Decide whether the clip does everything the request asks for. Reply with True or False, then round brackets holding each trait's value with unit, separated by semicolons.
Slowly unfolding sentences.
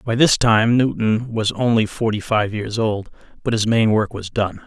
False (205 wpm)